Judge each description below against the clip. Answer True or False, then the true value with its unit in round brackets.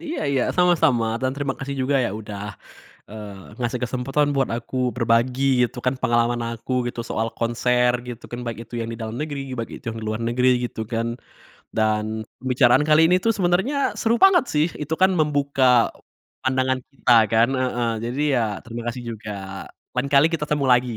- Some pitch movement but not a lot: True (3.3 semitones)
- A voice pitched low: True (125 Hz)